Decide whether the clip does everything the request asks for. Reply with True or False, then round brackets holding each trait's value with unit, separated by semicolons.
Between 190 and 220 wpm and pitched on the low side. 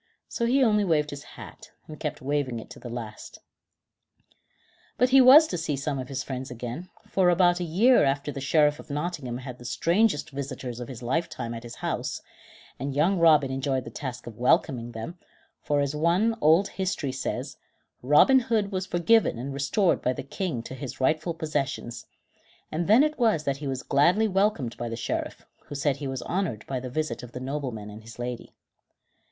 False (200 wpm; 145 Hz)